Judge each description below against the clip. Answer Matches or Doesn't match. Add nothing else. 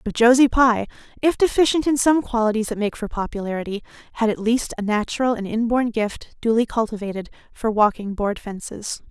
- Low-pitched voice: Doesn't match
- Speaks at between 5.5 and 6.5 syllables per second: Matches